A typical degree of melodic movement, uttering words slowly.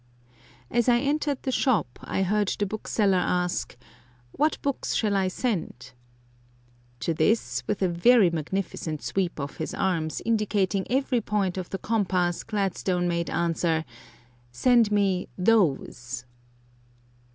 Yes: average, 4.4 semitones; slow, 130 wpm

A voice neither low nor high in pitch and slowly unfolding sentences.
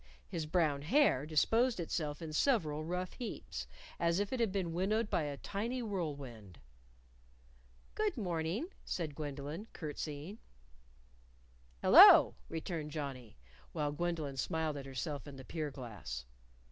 Yes: medium, 160 Hz; slow, 130 wpm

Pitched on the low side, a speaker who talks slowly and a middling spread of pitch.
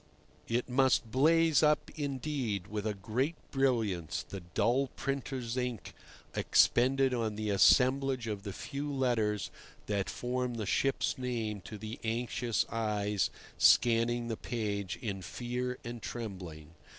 Yes: low, 120 Hz; slow, 130 wpm; average, 3.6 semitones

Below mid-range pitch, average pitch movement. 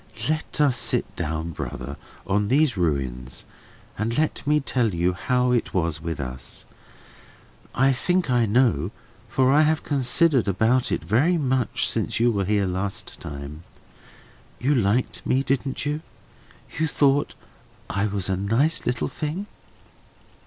No: low, 120 Hz; wide, 7.0 semitones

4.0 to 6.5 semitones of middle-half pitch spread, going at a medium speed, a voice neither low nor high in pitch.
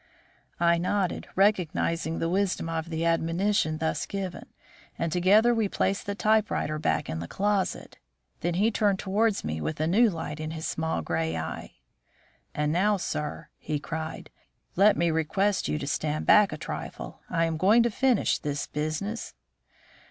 Yes: average, 4.5 semitones; average, 165 wpm; medium, 170 Hz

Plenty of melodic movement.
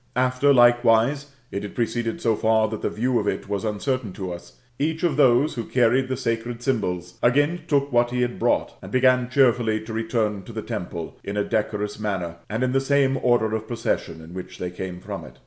No: average, 3.5 semitones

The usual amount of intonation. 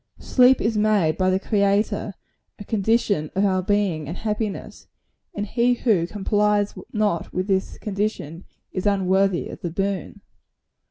No: narrow, 2.2 semitones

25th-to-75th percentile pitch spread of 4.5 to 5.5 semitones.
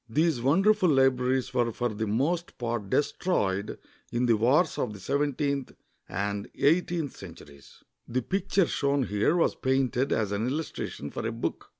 Yes: average, 5.1 semitones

